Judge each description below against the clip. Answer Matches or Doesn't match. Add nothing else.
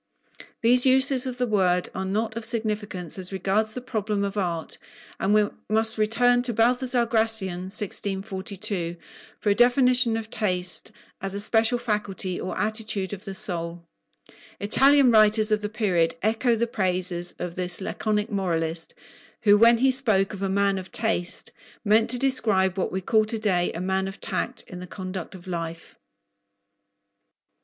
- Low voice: Doesn't match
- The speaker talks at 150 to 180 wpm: Matches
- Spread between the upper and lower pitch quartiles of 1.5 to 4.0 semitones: Matches